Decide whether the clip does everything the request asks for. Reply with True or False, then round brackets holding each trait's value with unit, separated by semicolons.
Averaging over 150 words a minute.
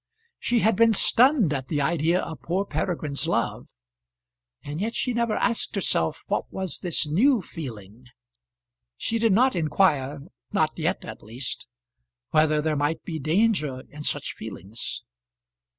False (145 wpm)